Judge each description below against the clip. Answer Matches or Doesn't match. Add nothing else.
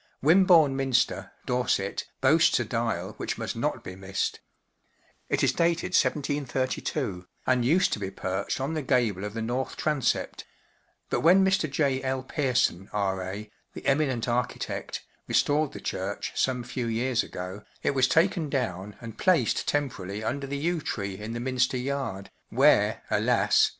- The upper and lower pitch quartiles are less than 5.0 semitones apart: Doesn't match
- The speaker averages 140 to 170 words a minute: Matches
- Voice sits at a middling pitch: Doesn't match